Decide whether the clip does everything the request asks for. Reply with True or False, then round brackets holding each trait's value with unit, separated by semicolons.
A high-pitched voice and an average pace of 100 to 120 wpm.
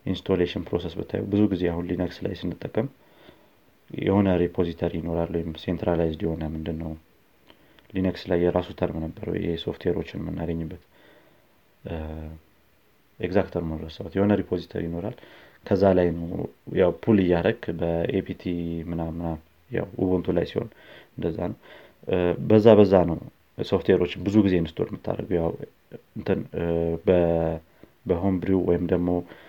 False (85 Hz; 110 wpm)